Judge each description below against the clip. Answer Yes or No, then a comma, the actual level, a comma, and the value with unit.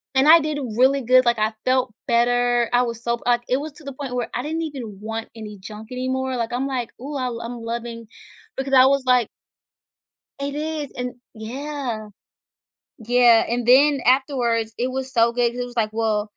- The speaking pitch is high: Yes, high, 245 Hz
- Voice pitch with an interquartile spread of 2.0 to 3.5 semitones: Yes, narrow, 2.4 semitones